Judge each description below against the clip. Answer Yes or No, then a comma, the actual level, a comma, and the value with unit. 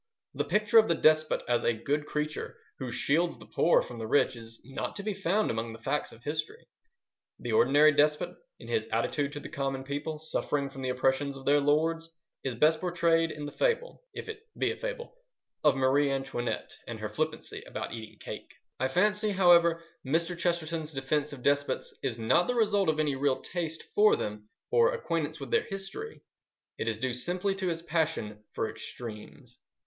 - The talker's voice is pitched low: No, medium, 150 Hz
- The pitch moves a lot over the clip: No, average, 4.7 semitones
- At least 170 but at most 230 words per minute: Yes, average, 185 wpm